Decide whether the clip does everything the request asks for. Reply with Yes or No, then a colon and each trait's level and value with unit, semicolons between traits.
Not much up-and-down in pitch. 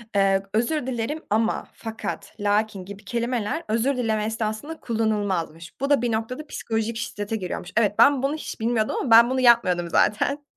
No: average, 3.1 semitones